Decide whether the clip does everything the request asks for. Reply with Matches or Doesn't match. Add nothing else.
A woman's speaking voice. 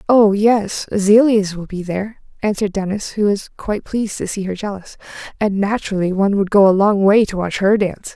Matches